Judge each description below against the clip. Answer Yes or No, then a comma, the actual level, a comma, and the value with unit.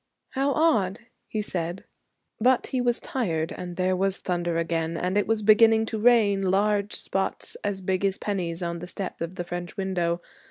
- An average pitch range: Yes, average, 3.5 semitones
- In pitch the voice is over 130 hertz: Yes, high, 190 Hz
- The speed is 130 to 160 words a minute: No, average, 185 wpm